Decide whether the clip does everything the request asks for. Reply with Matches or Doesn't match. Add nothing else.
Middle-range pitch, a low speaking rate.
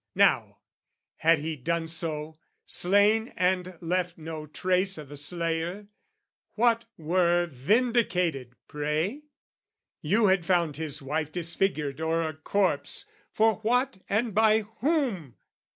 Matches